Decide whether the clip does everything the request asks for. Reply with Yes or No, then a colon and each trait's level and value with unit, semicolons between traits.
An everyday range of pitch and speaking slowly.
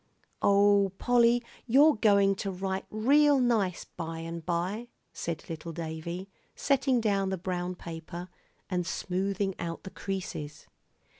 Yes: average, 4.1 semitones; slow, 130 wpm